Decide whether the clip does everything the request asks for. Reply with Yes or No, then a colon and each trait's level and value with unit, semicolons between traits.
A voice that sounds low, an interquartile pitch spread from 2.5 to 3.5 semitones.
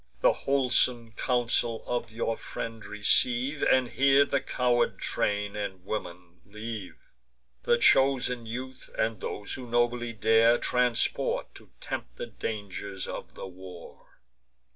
Yes: low, 115 Hz; average, 3.2 semitones